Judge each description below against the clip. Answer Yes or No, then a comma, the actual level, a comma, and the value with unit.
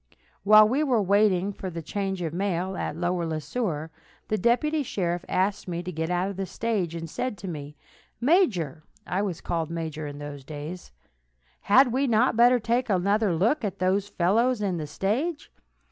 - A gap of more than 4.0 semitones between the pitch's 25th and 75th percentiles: Yes, average, 4.9 semitones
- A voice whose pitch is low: No, high, 190 Hz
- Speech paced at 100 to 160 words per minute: No, average, 180 wpm